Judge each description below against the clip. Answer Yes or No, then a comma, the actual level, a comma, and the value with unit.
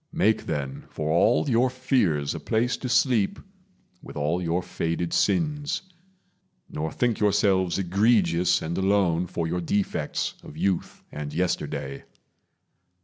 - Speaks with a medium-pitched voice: No, very low, 95 Hz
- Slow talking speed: Yes, slow, 130 wpm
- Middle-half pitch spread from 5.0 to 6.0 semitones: Yes, wide, 5.5 semitones